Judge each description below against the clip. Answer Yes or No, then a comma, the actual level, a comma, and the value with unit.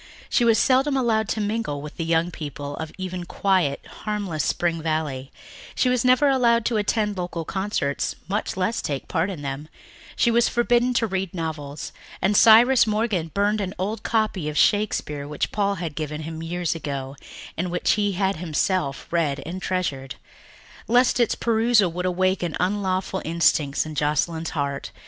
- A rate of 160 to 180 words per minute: Yes, average, 165 wpm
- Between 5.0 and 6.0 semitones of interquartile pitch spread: Yes, wide, 5.5 semitones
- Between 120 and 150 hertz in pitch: No, medium, 185 Hz